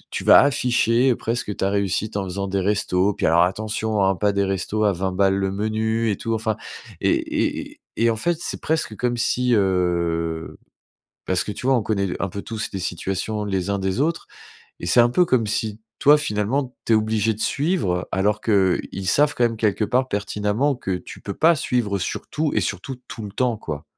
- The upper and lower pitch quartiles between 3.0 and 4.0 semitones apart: Yes, average, 3.4 semitones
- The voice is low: Yes, low, 105 Hz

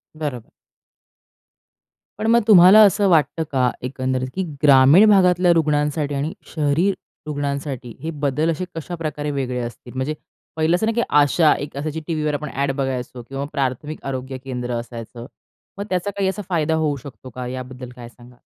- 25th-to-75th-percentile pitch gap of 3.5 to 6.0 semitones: Yes, average, 4.0 semitones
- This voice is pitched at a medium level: Yes, medium, 145 Hz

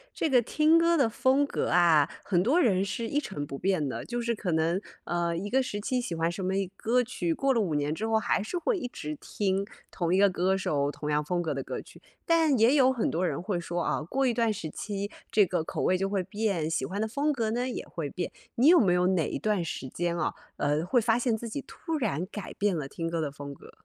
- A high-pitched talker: Yes, high, 195 Hz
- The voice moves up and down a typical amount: No, wide, 6.2 semitones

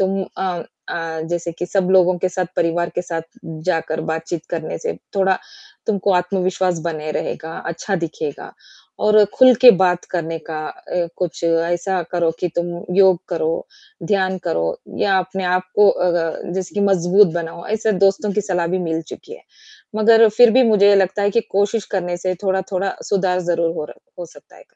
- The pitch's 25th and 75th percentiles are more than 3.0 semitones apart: No, narrow, 2.5 semitones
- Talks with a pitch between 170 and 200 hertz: Yes, medium, 185 Hz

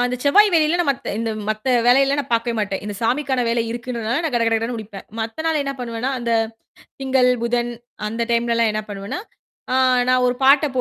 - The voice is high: Yes, high, 240 Hz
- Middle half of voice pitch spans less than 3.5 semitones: Yes, average, 2.9 semitones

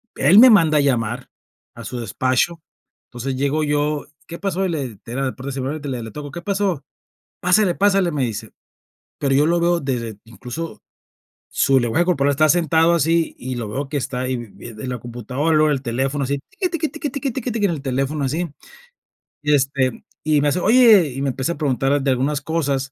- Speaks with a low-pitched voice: No, medium, 145 Hz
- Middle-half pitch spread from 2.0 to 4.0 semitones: No, average, 4.5 semitones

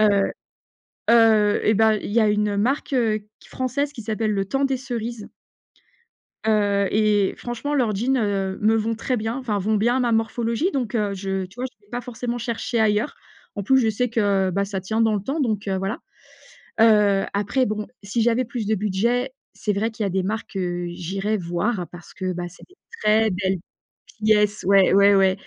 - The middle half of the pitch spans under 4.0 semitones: Yes, average, 3.0 semitones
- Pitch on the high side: Yes, high, 215 Hz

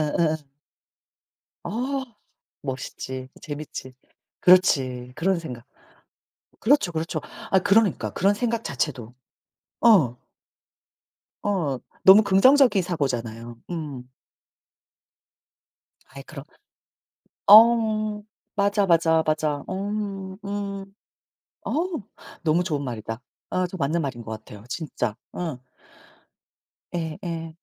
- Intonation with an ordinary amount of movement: No, wide, 6.5 semitones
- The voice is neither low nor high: Yes, medium, 165 Hz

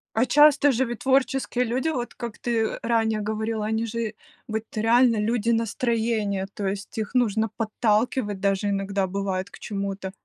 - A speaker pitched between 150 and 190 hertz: No, high, 220 Hz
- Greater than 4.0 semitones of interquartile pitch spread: No, average, 2.7 semitones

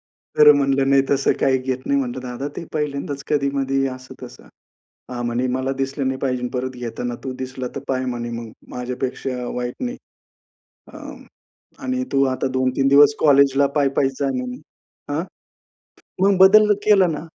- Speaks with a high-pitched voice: No, low, 135 Hz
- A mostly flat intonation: Yes, narrow, 1.9 semitones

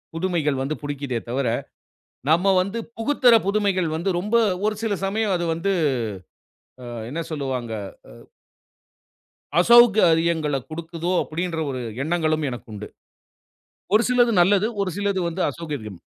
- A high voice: No, medium, 170 Hz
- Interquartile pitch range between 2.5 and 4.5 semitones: No, average, 5.1 semitones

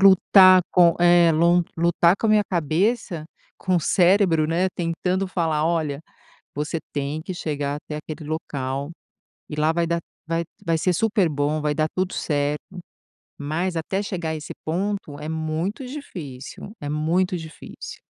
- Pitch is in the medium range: Yes, medium, 165 Hz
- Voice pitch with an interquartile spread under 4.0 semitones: Yes, average, 3.2 semitones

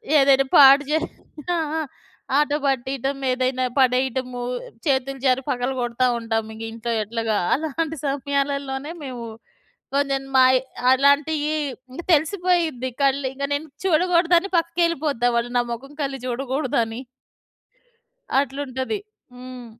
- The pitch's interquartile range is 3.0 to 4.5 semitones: No, narrow, 2.5 semitones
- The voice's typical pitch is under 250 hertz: No, very high, 270 Hz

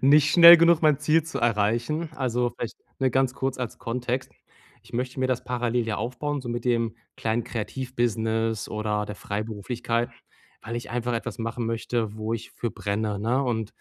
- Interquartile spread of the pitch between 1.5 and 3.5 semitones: Yes, narrow, 2.5 semitones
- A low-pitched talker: Yes, low, 120 Hz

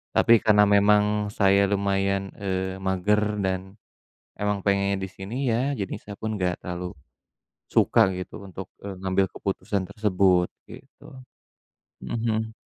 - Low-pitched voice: Yes, low, 100 Hz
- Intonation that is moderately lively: No, narrow, 1.7 semitones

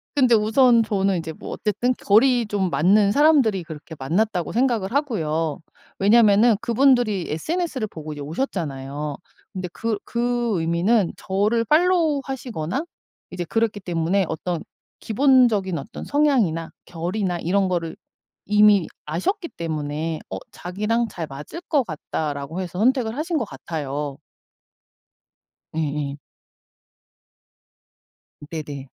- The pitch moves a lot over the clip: Yes, wide, 6.6 semitones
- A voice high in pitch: Yes, high, 195 Hz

